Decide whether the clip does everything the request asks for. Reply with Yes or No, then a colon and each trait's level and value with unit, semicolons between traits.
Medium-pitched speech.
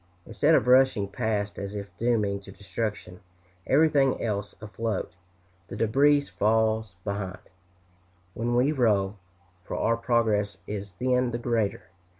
No: low, 110 Hz